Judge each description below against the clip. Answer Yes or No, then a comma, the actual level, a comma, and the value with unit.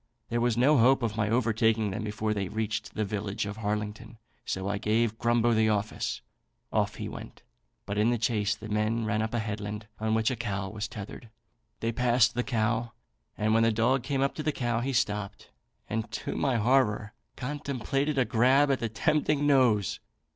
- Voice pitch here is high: No, low, 110 Hz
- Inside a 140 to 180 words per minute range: No, average, 195 wpm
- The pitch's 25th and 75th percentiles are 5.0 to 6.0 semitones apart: No, narrow, 2.4 semitones